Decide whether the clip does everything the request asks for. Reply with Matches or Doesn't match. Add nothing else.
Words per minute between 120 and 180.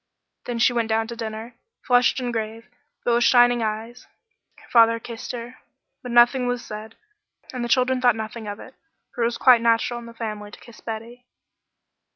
Doesn't match